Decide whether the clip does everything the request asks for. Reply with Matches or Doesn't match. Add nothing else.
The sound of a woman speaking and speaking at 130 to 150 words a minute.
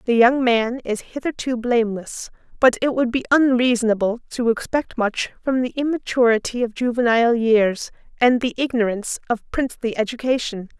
Matches